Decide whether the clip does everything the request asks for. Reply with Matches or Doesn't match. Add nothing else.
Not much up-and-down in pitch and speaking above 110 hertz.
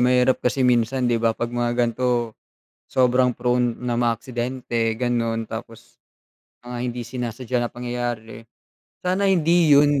Matches